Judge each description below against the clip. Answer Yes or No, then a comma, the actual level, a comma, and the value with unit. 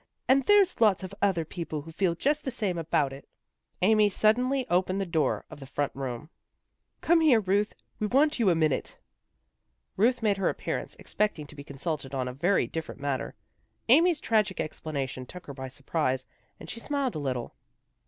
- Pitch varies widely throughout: Yes, wide, 7.8 semitones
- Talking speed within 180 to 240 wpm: Yes, average, 185 wpm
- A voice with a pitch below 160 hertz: No, medium, 180 Hz